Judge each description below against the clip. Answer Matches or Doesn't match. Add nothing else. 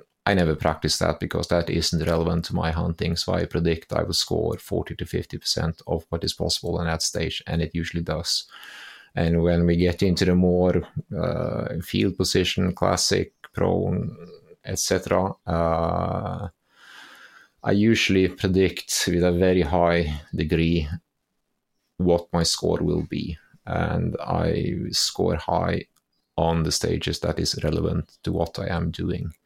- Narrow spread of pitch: Matches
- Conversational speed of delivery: Matches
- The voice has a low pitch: Matches